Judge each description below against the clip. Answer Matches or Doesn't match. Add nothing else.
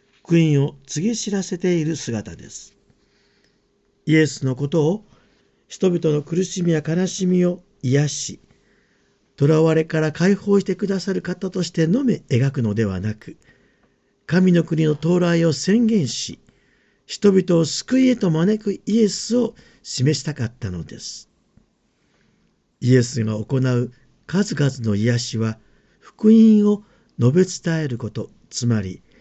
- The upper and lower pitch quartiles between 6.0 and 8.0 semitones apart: Matches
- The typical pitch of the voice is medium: Matches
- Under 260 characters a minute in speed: Matches